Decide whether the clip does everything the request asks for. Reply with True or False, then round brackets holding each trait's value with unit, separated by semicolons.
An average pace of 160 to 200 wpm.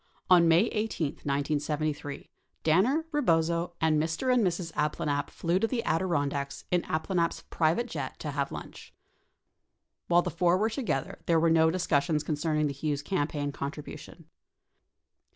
False (150 wpm)